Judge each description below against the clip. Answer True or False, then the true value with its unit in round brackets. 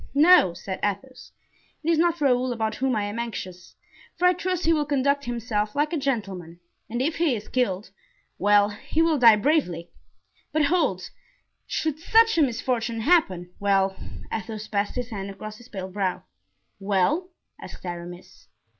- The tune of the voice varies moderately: False (6.8 semitones)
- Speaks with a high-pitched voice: True (230 Hz)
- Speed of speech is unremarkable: True (155 wpm)